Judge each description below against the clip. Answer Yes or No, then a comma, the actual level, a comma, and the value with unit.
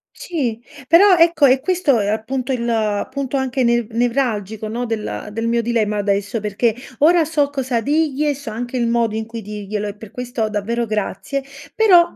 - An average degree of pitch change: Yes, average, 4.3 semitones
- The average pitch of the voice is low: No, high, 235 Hz